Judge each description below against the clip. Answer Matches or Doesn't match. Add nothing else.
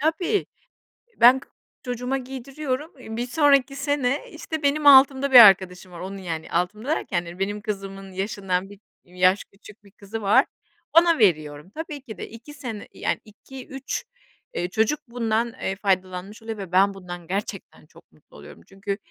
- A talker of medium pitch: Doesn't match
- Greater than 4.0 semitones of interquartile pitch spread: Matches